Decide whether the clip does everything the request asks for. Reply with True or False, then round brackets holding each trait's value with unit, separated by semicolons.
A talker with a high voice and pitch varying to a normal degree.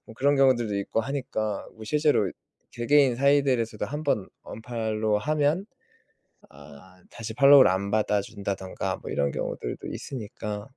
False (110 Hz; 5.0 semitones)